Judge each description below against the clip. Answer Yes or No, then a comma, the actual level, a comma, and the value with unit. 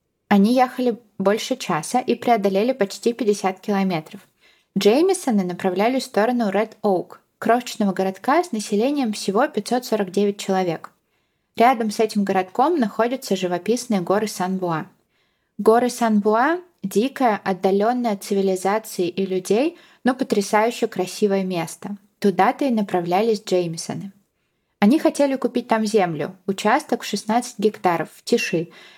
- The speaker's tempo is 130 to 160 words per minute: No, average, 120 wpm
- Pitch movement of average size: Yes, average, 3.6 semitones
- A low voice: No, high, 210 Hz